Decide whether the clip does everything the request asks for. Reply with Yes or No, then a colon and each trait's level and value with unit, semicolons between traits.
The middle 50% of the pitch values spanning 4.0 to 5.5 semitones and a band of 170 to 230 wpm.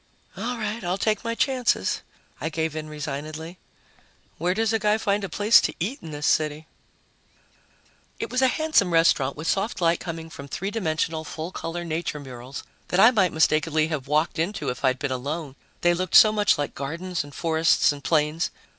Yes: average, 4.8 semitones; average, 190 wpm